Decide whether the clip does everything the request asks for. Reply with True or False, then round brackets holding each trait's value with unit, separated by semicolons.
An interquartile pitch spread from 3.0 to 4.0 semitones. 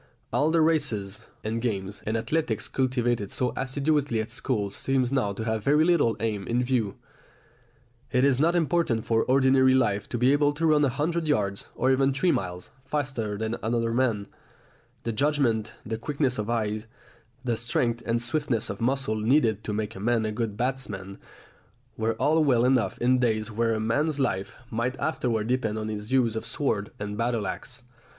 True (3.6 semitones)